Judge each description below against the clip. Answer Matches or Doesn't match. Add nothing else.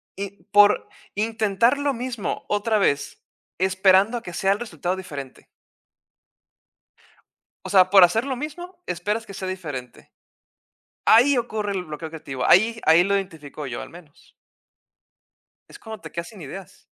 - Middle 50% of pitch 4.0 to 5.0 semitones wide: Matches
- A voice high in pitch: Matches